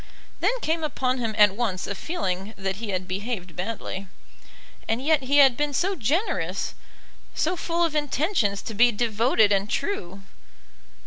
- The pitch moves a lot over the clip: Yes, wide, 6.9 semitones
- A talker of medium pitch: No, high, 230 Hz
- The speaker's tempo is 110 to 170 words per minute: Yes, average, 155 wpm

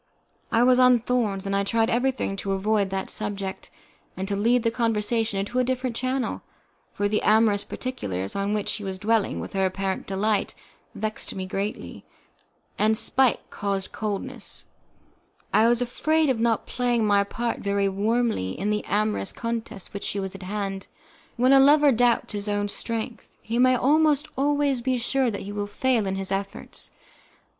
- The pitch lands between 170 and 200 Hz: No, high, 215 Hz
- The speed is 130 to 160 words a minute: No, average, 170 wpm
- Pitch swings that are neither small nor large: Yes, average, 3.7 semitones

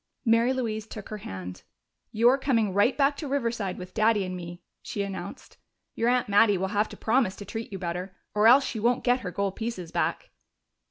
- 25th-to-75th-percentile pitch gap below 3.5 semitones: No, average, 3.8 semitones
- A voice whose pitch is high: Yes, high, 215 Hz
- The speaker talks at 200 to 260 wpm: Yes, fast, 205 wpm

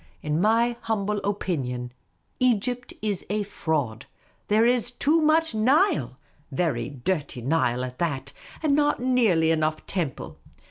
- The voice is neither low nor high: No, high, 195 Hz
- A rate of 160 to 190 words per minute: No, average, 140 wpm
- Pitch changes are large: Yes, wide, 9.0 semitones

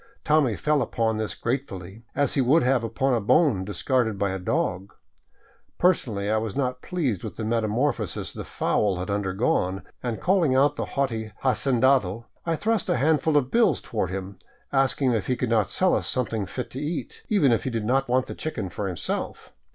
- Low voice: Yes, low, 120 Hz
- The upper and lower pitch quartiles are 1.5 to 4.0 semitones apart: No, average, 5.0 semitones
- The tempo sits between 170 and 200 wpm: Yes, average, 195 wpm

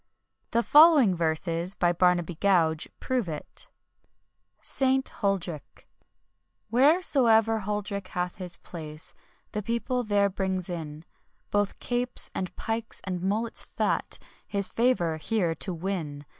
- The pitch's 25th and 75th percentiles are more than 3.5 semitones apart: Yes, average, 4.8 semitones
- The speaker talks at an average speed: No, slow, 115 wpm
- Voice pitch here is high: Yes, high, 195 Hz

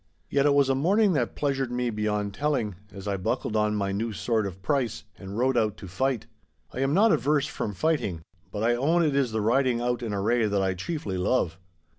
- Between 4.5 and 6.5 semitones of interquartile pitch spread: Yes, average, 5.1 semitones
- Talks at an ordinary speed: No, fast, 220 wpm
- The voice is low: Yes, low, 120 Hz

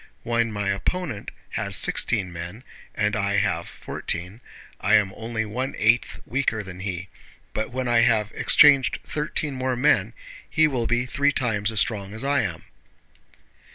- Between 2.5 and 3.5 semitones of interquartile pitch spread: No, average, 4.0 semitones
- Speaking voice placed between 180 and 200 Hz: No, low, 110 Hz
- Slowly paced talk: No, average, 155 wpm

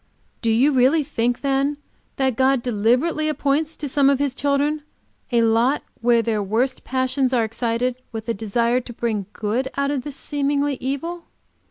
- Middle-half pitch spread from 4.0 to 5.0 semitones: No, average, 3.4 semitones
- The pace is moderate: Yes, average, 170 wpm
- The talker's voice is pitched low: No, very high, 260 Hz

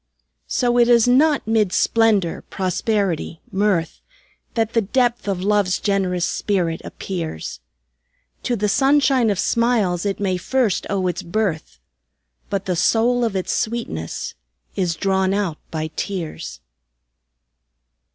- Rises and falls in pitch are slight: No, average, 4.2 semitones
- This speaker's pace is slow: Yes, slow, 125 wpm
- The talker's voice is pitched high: Yes, high, 200 Hz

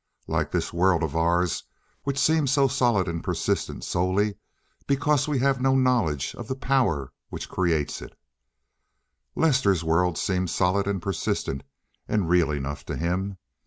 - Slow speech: No, average, 150 wpm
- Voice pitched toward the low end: Yes, very low, 95 Hz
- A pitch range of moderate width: No, wide, 7.6 semitones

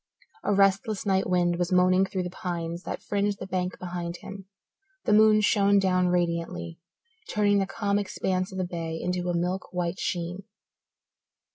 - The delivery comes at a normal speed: Yes, average, 165 wpm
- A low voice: No, medium, 185 Hz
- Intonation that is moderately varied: No, narrow, 2.1 semitones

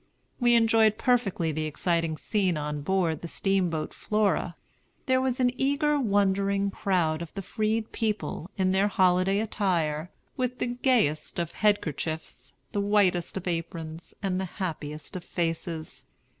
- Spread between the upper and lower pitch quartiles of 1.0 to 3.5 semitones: No, average, 4.5 semitones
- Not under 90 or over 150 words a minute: Yes, average, 145 wpm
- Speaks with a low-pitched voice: No, high, 190 Hz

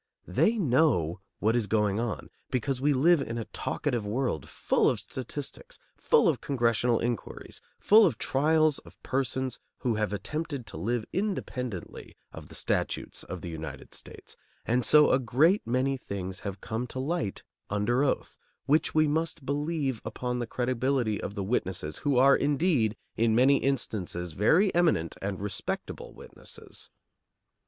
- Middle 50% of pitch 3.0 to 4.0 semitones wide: No, average, 5.2 semitones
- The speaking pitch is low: Yes, low, 125 Hz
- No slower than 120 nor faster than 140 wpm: No, average, 155 wpm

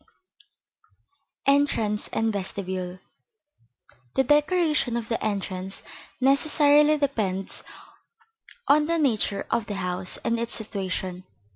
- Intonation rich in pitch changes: Yes, wide, 6.8 semitones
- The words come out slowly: Yes, slow, 105 wpm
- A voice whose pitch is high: Yes, high, 225 Hz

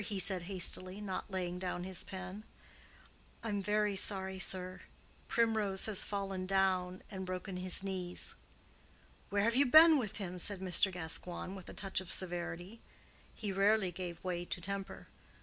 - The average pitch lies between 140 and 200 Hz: Yes, high, 190 Hz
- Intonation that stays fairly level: Yes, narrow, 1.8 semitones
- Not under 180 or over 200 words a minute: No, average, 155 wpm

